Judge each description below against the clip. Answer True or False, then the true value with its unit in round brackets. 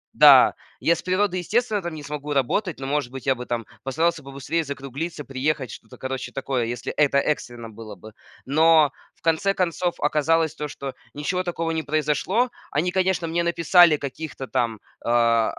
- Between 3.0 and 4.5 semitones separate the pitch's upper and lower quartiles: True (4.1 semitones)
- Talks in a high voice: False (150 Hz)